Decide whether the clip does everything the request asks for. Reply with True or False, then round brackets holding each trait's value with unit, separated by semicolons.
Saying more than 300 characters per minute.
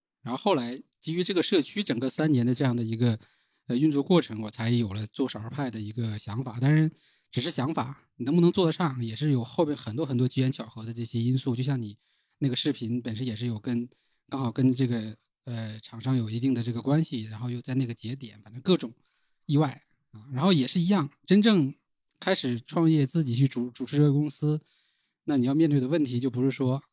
True (325 characters per minute)